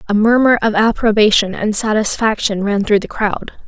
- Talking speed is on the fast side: No, average, 165 wpm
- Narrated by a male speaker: No, female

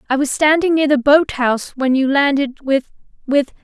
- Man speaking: No, female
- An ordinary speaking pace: Yes, average, 180 wpm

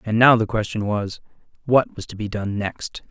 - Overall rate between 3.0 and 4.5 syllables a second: No, 4.8 syllables/s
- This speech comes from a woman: No, male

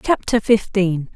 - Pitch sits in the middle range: No, high, 200 Hz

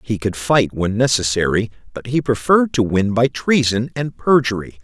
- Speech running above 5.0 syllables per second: No, 4.9 syllables/s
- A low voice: Yes, low, 115 Hz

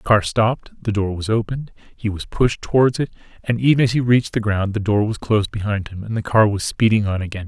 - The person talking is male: Yes, male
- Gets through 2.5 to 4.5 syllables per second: No, 6.1 syllables/s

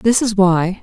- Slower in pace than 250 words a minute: Yes, fast, 220 wpm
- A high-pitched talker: Yes, high, 205 Hz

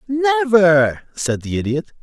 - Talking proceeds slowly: Yes, slow, 120 wpm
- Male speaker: Yes, male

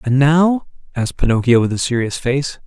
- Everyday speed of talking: Yes, average, 180 wpm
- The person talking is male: Yes, male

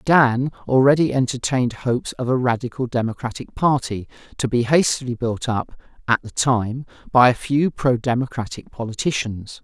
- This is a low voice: Yes, low, 125 Hz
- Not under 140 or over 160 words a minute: Yes, average, 145 wpm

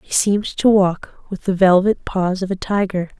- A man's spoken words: No, female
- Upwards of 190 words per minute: Yes, fast, 205 wpm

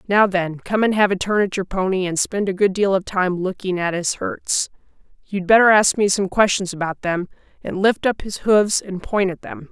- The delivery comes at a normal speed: No, fast, 235 wpm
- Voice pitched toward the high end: Yes, high, 195 Hz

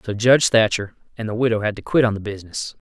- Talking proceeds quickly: Yes, fast, 250 wpm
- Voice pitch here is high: No, low, 110 Hz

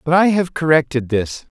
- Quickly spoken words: No, average, 190 wpm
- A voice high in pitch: No, medium, 155 Hz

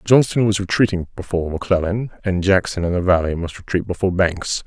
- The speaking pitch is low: Yes, very low, 95 Hz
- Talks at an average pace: Yes, average, 180 wpm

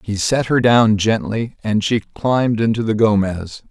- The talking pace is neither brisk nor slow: Yes, average, 180 wpm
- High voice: No, low, 110 Hz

